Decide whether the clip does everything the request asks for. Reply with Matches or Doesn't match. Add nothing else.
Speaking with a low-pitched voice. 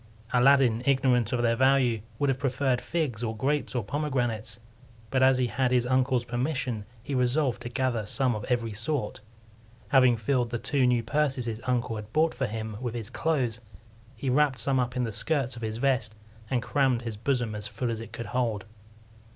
Matches